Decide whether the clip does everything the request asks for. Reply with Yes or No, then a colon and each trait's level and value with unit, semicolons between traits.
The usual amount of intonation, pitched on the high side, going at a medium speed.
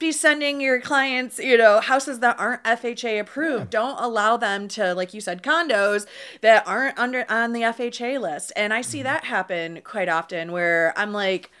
Yes: average, 4.1 semitones; high, 225 Hz; average, 185 wpm